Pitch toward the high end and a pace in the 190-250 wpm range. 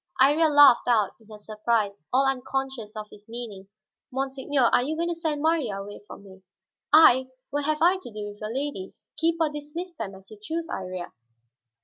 Yes: very high, 260 Hz; average, 195 wpm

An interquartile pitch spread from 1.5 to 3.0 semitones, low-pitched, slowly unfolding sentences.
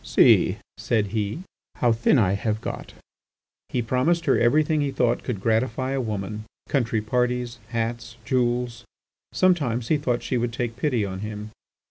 No: narrow, 2.6 semitones; low, 120 Hz; average, 155 wpm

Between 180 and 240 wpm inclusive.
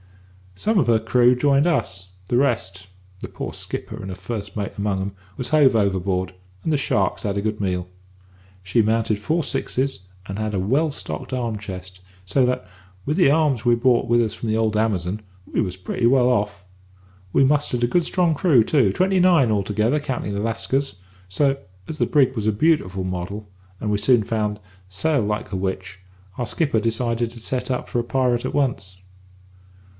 Yes: average, 190 wpm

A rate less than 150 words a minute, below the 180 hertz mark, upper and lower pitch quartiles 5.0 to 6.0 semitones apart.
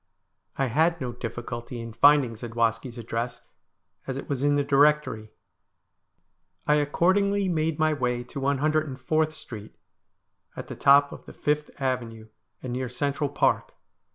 No: average, 140 wpm; low, 135 Hz; average, 3.9 semitones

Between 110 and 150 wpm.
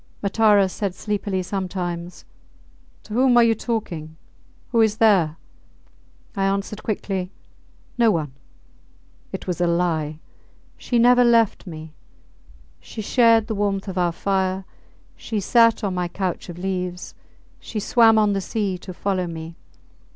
Yes: average, 140 wpm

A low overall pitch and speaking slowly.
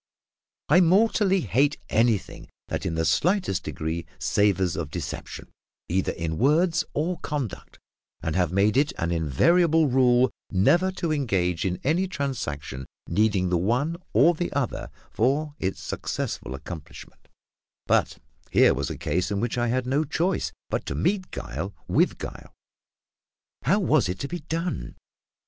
No: low, 125 Hz; average, 150 wpm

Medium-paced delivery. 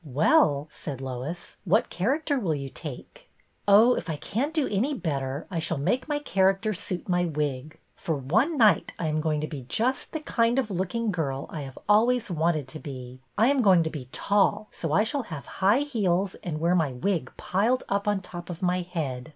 No: fast, 215 wpm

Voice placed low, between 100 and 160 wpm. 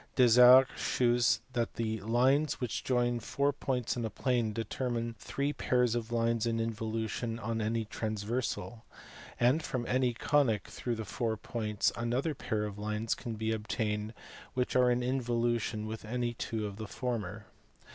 Yes: low, 115 Hz; average, 155 wpm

